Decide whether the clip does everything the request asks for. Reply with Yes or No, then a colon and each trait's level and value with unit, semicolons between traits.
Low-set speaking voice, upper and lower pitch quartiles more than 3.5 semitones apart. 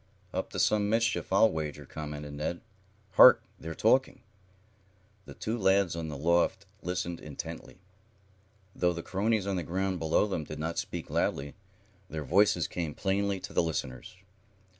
Yes: very low, 85 Hz; average, 4.1 semitones